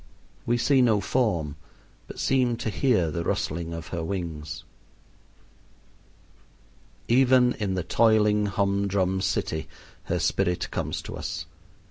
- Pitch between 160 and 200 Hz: No, low, 100 Hz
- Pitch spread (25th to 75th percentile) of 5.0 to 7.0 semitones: Yes, wide, 5.6 semitones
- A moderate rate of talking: No, slow, 125 wpm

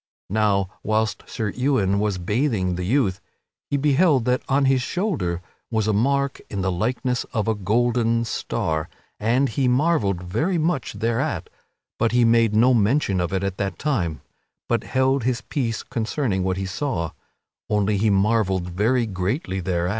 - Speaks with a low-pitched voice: Yes, low, 110 Hz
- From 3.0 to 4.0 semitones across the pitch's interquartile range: No, average, 5.1 semitones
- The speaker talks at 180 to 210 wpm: No, average, 160 wpm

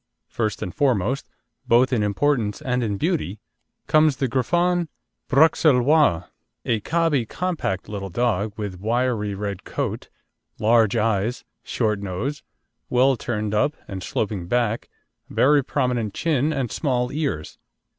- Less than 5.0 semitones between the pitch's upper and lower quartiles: No, average, 5.3 semitones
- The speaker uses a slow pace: Yes, slow, 125 wpm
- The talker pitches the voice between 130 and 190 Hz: No, low, 120 Hz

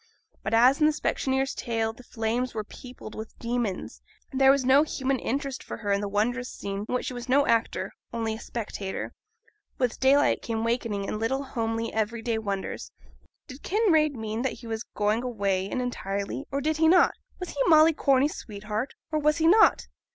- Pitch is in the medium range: No, high, 245 Hz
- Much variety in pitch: No, average, 3.8 semitones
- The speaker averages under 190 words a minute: No, average, 195 wpm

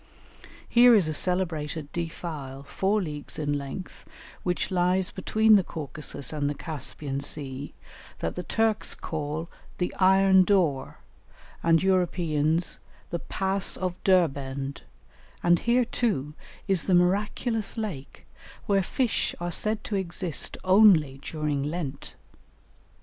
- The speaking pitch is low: No, medium, 175 Hz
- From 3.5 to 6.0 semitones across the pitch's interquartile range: Yes, average, 4.6 semitones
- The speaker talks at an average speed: No, slow, 120 wpm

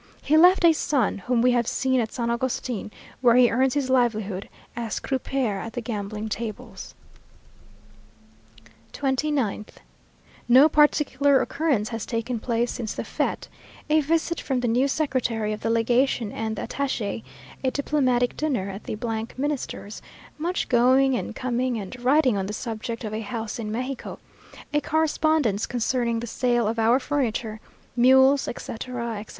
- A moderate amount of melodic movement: Yes, average, 3.2 semitones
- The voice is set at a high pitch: Yes, high, 245 Hz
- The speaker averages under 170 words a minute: Yes, average, 150 wpm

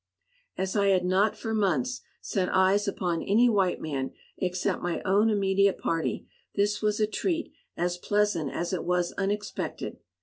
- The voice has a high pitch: Yes, high, 195 Hz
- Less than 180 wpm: Yes, average, 160 wpm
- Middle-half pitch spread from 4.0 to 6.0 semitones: No, average, 2.8 semitones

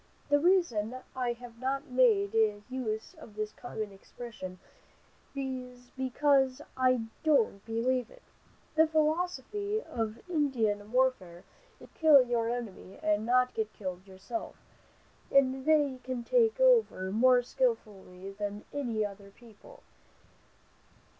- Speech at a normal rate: No, slow, 120 wpm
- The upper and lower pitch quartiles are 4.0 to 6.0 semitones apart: Yes, average, 4.7 semitones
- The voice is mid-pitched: No, very high, 250 Hz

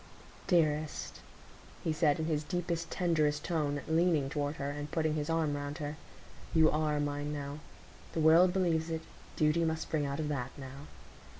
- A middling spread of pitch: No, narrow, 1.9 semitones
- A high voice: No, medium, 155 Hz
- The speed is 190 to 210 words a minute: No, average, 165 wpm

